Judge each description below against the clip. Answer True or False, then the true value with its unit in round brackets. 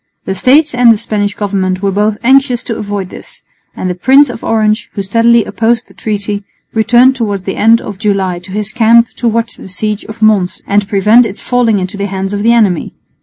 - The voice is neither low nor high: False (215 Hz)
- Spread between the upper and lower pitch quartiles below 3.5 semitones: True (2.7 semitones)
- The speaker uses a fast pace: True (215 wpm)